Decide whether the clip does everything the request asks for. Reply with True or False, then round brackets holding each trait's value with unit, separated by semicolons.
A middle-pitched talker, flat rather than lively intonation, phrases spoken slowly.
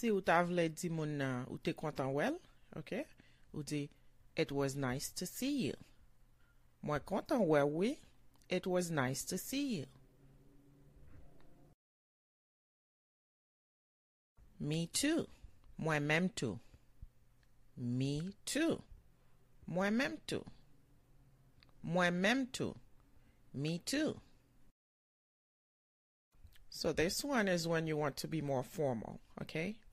False (150 Hz; 5.5 semitones; 100 wpm)